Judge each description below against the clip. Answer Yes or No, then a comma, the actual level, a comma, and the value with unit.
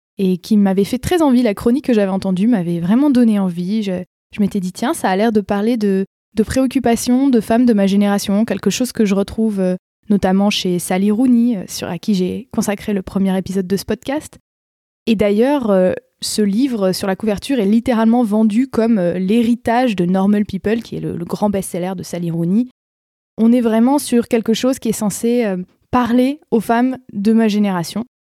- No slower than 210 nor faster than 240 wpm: No, average, 195 wpm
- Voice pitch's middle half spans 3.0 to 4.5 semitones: Yes, average, 3.4 semitones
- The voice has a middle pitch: No, high, 215 Hz